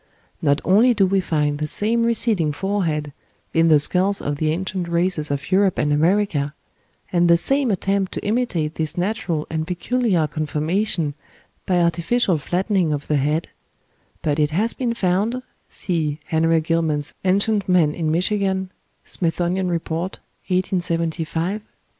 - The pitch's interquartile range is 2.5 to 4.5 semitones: Yes, average, 4.0 semitones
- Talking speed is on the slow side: No, average, 145 wpm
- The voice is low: No, medium, 175 Hz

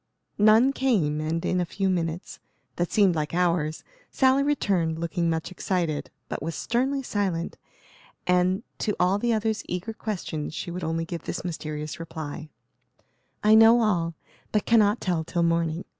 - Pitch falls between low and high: Yes, medium, 180 Hz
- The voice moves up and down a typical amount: Yes, average, 4.5 semitones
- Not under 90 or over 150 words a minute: No, average, 160 wpm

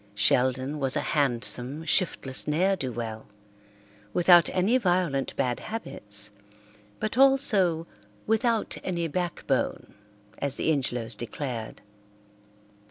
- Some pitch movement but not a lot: No, wide, 6.7 semitones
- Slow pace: Yes, slow, 100 wpm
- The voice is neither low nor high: Yes, medium, 150 Hz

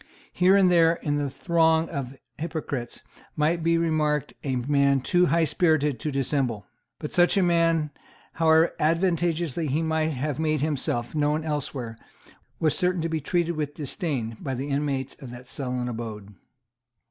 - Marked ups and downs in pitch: No, average, 3.4 semitones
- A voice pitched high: No, medium, 150 Hz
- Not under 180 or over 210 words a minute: No, average, 155 wpm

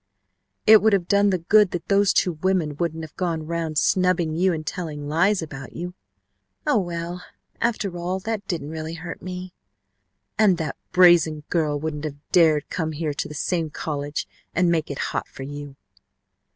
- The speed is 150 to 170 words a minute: No, average, 185 wpm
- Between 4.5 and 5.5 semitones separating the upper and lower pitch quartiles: No, average, 3.2 semitones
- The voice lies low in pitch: No, medium, 165 Hz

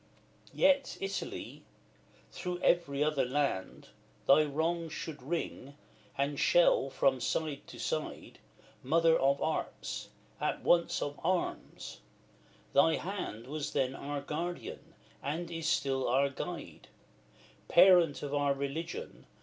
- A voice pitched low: No, medium, 150 Hz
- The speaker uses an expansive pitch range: No, average, 3.5 semitones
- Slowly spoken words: Yes, slow, 120 wpm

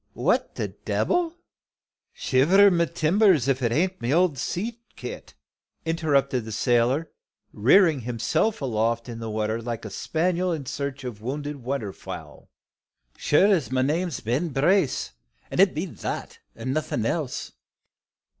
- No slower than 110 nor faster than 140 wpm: Yes, slow, 135 wpm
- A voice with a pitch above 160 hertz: No, medium, 140 Hz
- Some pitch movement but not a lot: No, wide, 6.3 semitones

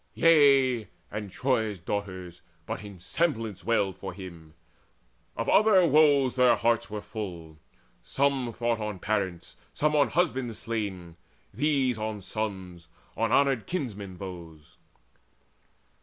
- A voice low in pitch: Yes, low, 110 Hz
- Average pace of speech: No, slow, 125 wpm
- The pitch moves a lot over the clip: Yes, wide, 5.9 semitones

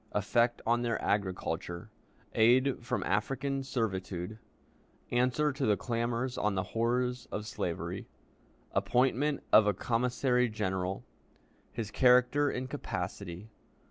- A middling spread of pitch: Yes, average, 3.4 semitones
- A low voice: Yes, low, 120 Hz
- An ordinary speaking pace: No, slow, 110 wpm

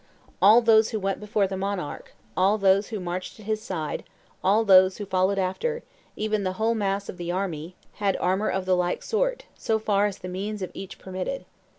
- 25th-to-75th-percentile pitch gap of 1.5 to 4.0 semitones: Yes, narrow, 2.4 semitones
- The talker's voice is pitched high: Yes, high, 195 Hz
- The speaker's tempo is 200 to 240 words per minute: Yes, fast, 205 wpm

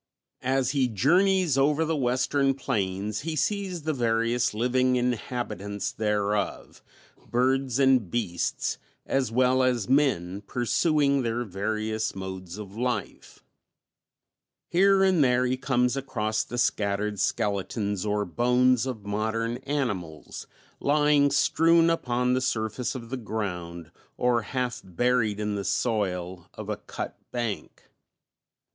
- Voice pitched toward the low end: Yes, low, 120 Hz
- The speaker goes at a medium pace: No, slow, 125 wpm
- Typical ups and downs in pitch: Yes, average, 4.2 semitones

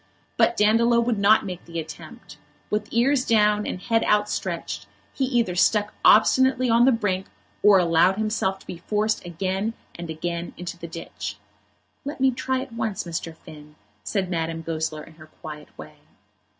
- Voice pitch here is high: Yes, high, 200 Hz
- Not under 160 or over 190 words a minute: Yes, average, 165 wpm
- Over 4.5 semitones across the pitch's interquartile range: Yes, average, 5.2 semitones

